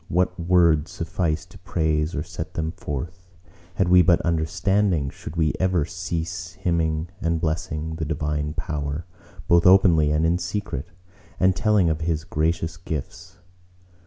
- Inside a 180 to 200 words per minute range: No, average, 145 wpm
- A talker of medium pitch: No, very low, 85 Hz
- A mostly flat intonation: Yes, narrow, 2.3 semitones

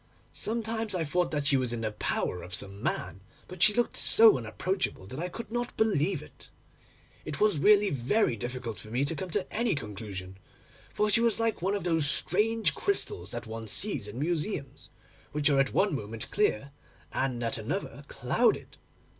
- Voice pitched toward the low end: No, medium, 155 Hz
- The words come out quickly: No, average, 185 wpm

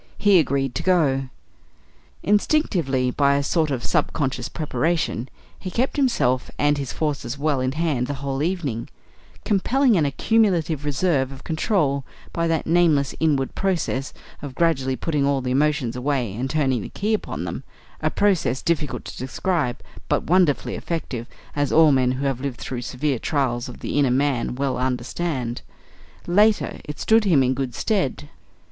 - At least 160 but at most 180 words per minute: Yes, average, 165 wpm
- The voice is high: No, medium, 145 Hz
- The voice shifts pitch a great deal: No, average, 4.3 semitones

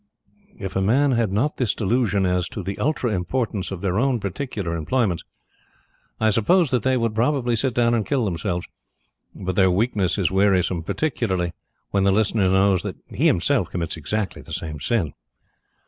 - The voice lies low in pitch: Yes, low, 100 Hz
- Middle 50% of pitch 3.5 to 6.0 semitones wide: Yes, average, 4.3 semitones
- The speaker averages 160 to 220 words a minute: Yes, average, 165 wpm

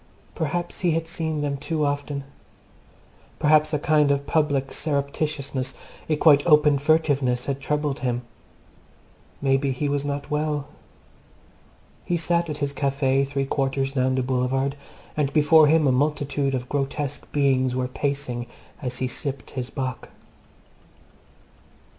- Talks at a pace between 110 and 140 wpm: Yes, slow, 135 wpm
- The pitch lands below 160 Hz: Yes, medium, 140 Hz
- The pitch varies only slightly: Yes, narrow, 2.0 semitones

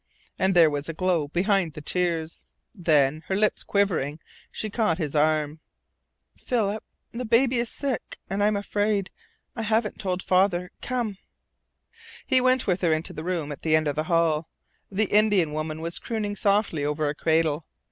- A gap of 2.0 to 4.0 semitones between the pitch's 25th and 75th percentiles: No, average, 5.0 semitones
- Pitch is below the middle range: No, medium, 180 Hz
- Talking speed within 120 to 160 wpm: No, average, 175 wpm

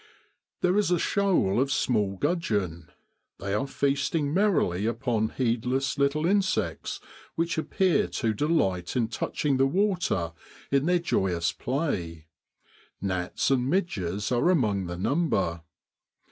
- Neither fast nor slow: No, slow, 130 wpm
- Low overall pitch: Yes, low, 130 Hz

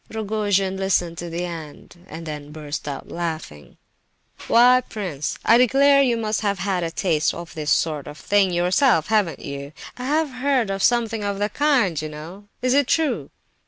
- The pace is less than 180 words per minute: No, average, 185 wpm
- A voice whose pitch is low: No, high, 195 Hz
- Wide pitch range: Yes, wide, 6.3 semitones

